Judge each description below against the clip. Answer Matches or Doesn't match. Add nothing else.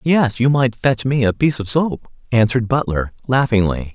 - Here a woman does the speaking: Doesn't match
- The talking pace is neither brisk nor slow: Matches